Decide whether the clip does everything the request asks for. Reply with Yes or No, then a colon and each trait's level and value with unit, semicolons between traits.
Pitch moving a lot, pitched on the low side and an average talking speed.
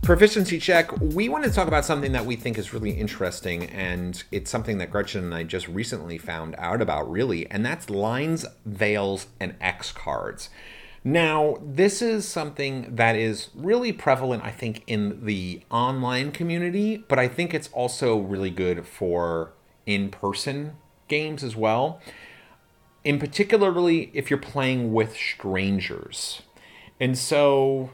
Yes: wide, 7.0 semitones; low, 125 Hz; average, 150 wpm